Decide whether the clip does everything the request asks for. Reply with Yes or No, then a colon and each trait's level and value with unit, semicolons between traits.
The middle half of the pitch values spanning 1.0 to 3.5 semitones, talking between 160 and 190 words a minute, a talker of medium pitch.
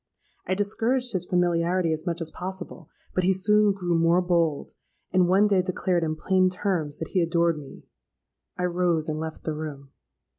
Yes: narrow, 2.4 semitones; average, 180 wpm; medium, 175 Hz